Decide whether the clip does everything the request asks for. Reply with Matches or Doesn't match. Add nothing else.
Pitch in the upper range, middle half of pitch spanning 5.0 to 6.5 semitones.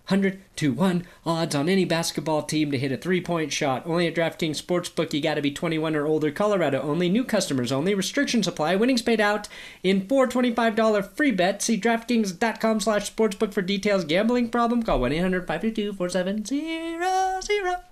Matches